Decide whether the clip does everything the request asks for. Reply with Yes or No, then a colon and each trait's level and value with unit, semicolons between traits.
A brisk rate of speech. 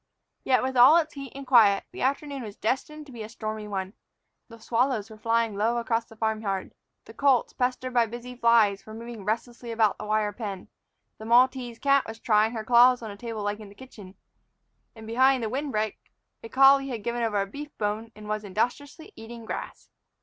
Yes: fast, 210 wpm